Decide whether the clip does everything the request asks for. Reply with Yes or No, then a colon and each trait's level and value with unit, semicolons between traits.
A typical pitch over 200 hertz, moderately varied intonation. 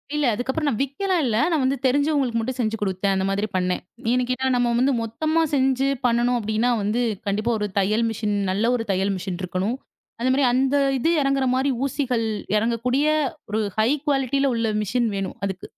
Yes: high, 240 Hz; average, 4.1 semitones